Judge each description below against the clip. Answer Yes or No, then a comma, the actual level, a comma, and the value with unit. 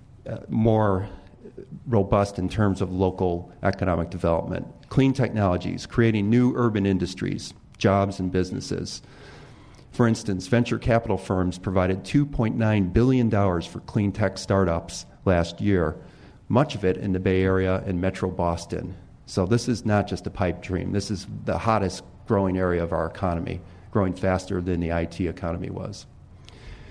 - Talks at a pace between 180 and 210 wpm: No, average, 145 wpm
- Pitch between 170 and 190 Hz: No, very low, 95 Hz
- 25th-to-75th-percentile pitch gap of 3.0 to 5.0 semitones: Yes, average, 3.5 semitones